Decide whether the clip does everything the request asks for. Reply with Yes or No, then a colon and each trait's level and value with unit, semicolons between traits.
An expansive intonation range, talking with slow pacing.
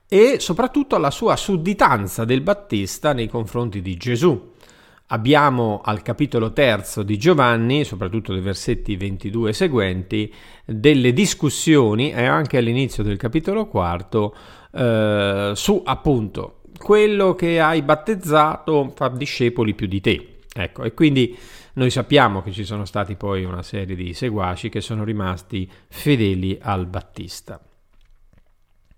No: wide, 6.5 semitones; average, 130 wpm